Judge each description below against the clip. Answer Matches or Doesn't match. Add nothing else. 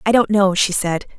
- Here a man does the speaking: Doesn't match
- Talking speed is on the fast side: Matches